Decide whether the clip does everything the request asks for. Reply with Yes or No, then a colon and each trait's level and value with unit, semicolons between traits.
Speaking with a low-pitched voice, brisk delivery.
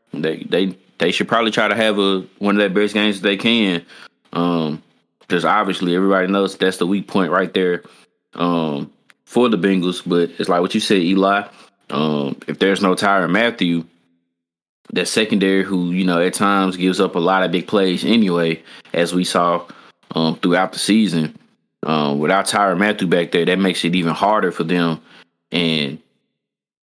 No: very low, 90 Hz; average, 180 wpm